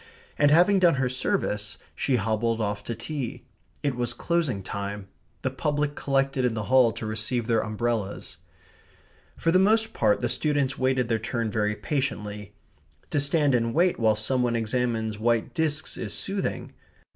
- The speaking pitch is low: Yes, low, 120 Hz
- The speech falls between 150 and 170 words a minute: Yes, average, 165 wpm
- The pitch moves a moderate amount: Yes, average, 4.9 semitones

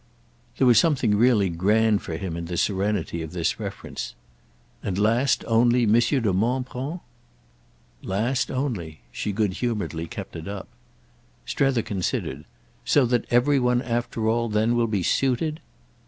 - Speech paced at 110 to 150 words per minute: Yes, average, 140 wpm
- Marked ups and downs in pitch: No, average, 4.3 semitones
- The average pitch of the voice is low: Yes, low, 110 Hz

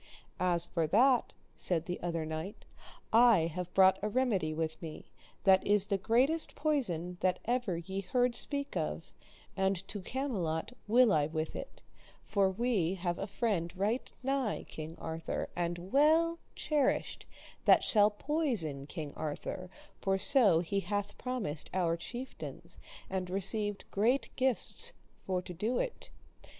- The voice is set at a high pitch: Yes, high, 195 Hz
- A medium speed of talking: Yes, average, 145 wpm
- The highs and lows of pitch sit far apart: Yes, wide, 6.1 semitones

